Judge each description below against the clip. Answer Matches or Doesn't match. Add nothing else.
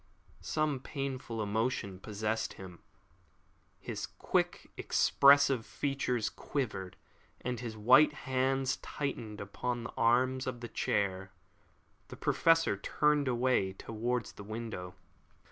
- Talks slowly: Matches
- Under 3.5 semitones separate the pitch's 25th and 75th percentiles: Doesn't match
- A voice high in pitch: Doesn't match